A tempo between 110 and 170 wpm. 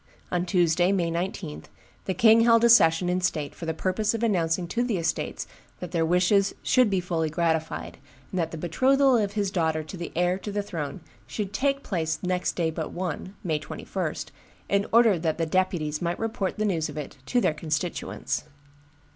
No: average, 195 wpm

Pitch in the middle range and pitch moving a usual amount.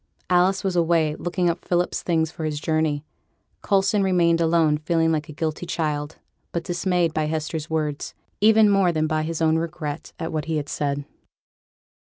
No: medium, 160 Hz; narrow, 2.1 semitones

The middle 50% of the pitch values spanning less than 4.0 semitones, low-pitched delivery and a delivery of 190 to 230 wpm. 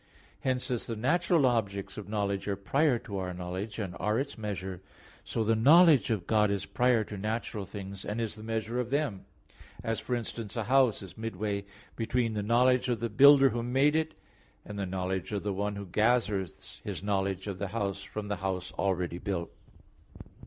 Yes: average, 3.5 semitones; low, 105 Hz; average, 195 wpm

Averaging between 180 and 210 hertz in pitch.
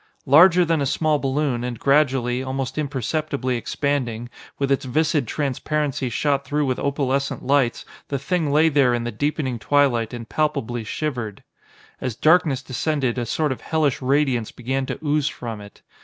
No: low, 135 Hz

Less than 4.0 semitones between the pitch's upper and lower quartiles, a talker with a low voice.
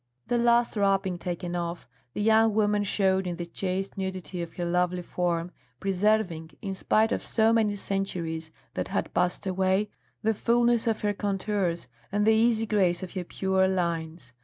No: average, 3.1 semitones; high, 190 Hz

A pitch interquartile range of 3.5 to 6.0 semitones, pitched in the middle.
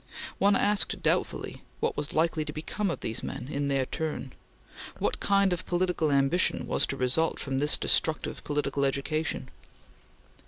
Yes: average, 4.0 semitones; medium, 155 Hz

